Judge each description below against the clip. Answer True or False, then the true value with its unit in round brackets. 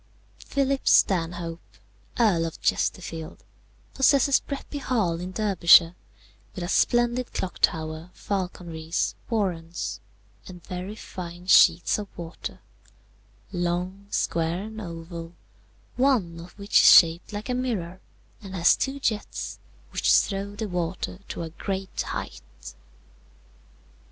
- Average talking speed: False (115 wpm)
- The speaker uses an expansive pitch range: False (4.0 semitones)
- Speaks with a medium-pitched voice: True (180 Hz)